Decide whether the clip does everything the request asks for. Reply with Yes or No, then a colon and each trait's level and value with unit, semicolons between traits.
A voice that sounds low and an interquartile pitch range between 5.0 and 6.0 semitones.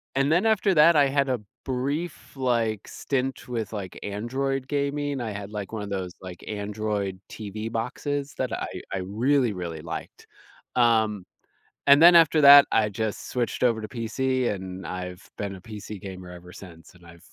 Yes: low, 110 Hz; wide, 5.6 semitones